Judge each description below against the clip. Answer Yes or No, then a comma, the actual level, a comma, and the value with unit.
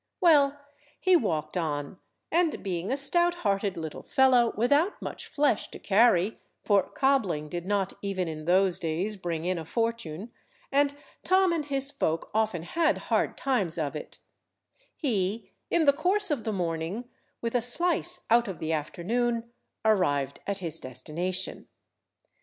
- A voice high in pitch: Yes, high, 210 Hz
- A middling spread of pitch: No, wide, 8.2 semitones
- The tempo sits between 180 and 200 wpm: No, average, 150 wpm